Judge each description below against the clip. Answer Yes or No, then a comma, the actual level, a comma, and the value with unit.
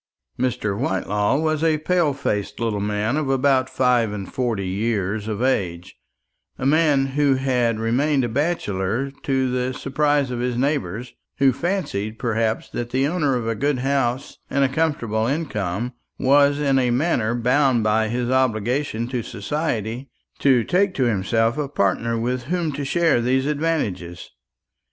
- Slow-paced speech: No, average, 155 wpm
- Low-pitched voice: Yes, low, 125 Hz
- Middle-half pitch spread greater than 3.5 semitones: Yes, average, 4.0 semitones